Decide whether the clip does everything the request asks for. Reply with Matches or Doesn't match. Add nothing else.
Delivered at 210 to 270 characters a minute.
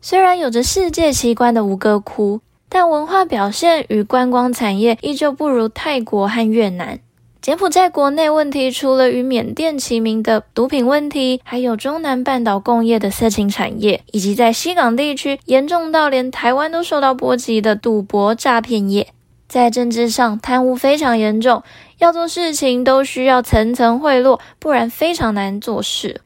Matches